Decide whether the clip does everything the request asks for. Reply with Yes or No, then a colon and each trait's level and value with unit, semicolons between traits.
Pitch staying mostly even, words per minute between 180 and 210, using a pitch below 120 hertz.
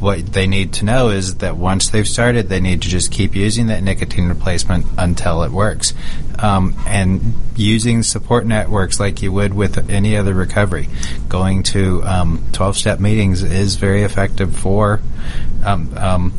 No: narrow, 2.2 semitones; average, 165 wpm; low, 100 Hz